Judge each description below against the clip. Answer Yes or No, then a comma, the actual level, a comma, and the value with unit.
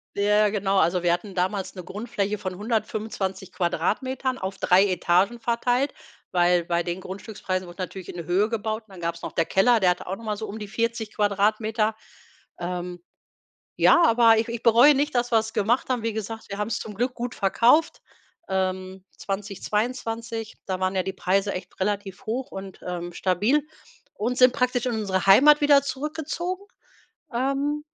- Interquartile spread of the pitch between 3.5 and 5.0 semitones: Yes, average, 3.9 semitones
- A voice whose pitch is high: Yes, high, 210 Hz